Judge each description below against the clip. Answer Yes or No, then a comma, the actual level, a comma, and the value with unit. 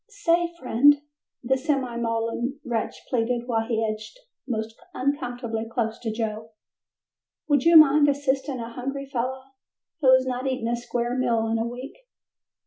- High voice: Yes, high, 245 Hz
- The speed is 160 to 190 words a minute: No, average, 150 wpm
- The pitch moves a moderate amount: Yes, average, 3.1 semitones